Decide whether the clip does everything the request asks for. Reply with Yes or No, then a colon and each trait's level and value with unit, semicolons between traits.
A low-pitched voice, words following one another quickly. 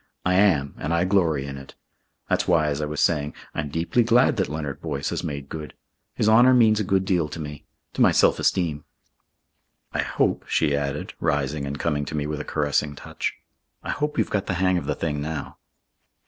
Yes: very low, 75 Hz; fast, 210 wpm